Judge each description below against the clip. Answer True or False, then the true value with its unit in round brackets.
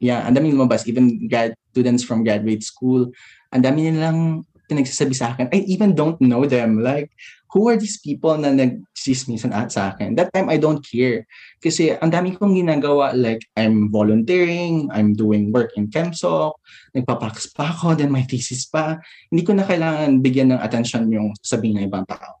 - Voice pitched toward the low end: True (130 Hz)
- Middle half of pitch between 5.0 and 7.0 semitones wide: True (5.5 semitones)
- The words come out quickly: True (180 wpm)